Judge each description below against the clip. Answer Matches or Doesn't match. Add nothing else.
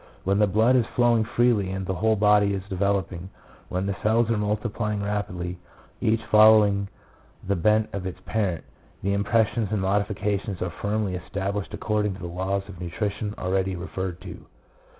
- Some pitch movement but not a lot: Doesn't match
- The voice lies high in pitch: Doesn't match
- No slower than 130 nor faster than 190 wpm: Matches